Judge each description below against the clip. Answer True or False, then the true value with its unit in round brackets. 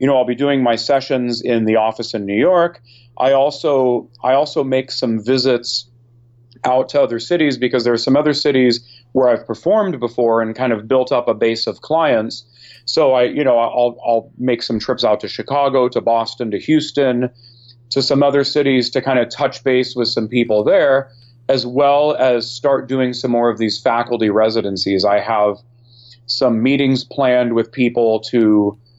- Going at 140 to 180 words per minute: False (190 wpm)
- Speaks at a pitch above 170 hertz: False (120 Hz)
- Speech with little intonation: True (2.2 semitones)